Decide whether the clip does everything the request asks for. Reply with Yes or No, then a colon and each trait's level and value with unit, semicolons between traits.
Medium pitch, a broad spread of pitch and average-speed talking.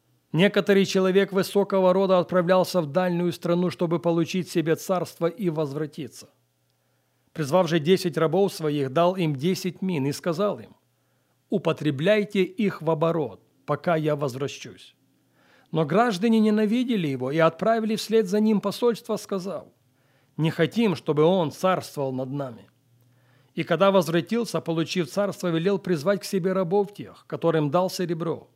No: medium, 175 Hz; average, 4.3 semitones; average, 135 wpm